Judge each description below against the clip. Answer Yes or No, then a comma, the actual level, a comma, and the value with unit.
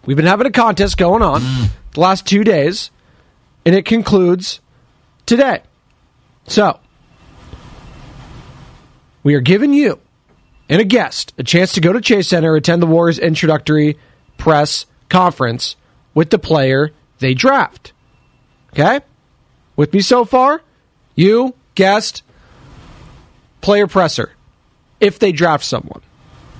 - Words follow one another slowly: Yes, slow, 120 wpm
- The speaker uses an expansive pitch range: Yes, wide, 5.7 semitones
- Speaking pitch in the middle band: Yes, medium, 175 Hz